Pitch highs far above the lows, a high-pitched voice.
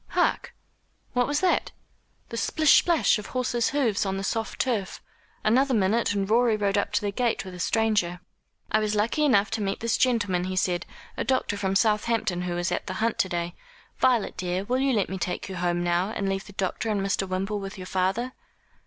No: average, 3.6 semitones; high, 205 Hz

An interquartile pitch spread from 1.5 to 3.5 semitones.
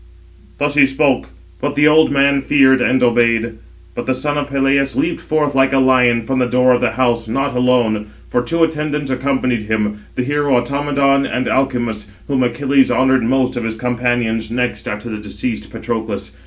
Yes: average, 2.8 semitones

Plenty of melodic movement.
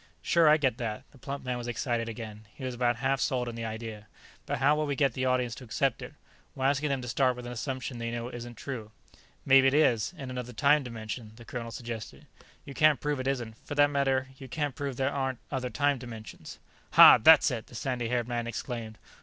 No: average, 2.7 semitones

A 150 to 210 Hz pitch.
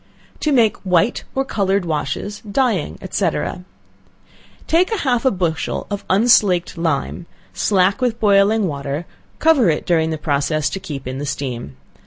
Yes: high, 190 Hz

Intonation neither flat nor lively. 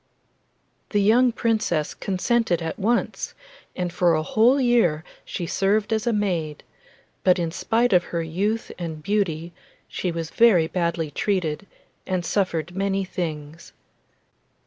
Yes: average, 4.4 semitones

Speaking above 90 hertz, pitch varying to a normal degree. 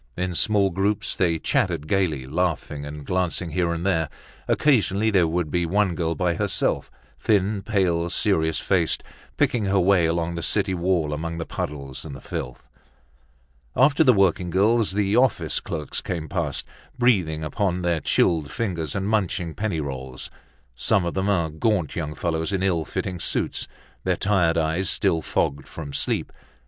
No: very low, 85 Hz; average, 3.5 semitones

